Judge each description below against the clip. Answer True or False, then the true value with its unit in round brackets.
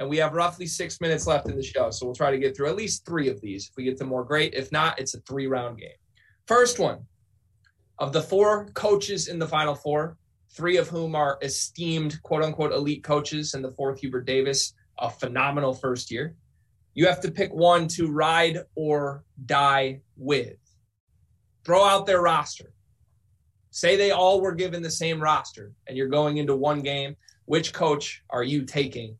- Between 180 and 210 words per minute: True (195 wpm)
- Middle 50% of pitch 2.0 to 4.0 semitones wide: False (4.4 semitones)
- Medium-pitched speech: True (145 Hz)